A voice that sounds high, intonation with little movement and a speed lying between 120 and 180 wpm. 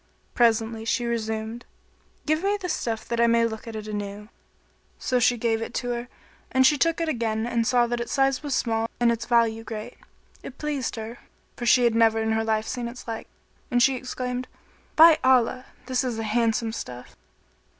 No: high, 235 Hz; narrow, 2.2 semitones; average, 195 wpm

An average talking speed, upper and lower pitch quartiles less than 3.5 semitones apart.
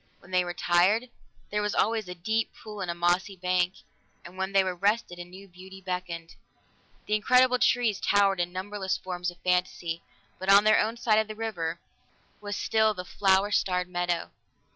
Yes: average, 185 wpm; average, 2.8 semitones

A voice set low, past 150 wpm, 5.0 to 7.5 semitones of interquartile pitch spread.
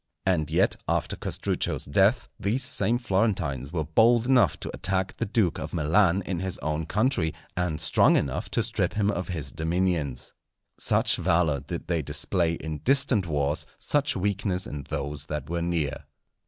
No: very low, 90 Hz; average, 165 wpm; average, 4.6 semitones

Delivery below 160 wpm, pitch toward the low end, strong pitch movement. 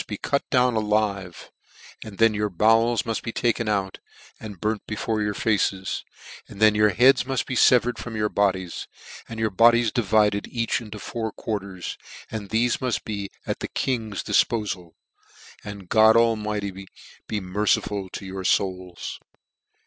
No: average, 150 wpm; low, 105 Hz; narrow, 2.5 semitones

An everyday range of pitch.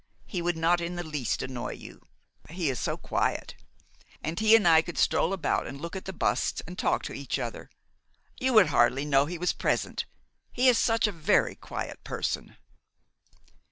Yes: average, 4.4 semitones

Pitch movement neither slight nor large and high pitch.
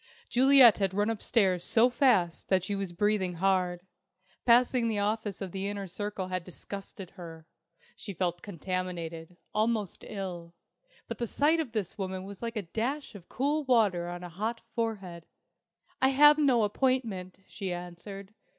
Yes: average, 4.2 semitones; high, 200 Hz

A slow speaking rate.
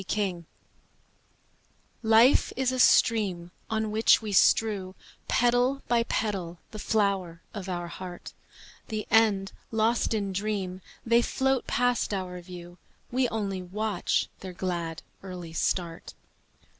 Yes: slow, 120 wpm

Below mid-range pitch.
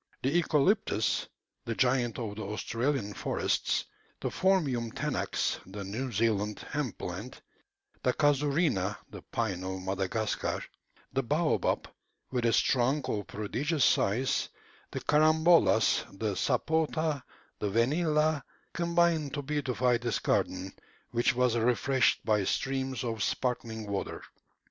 Yes: low, 125 Hz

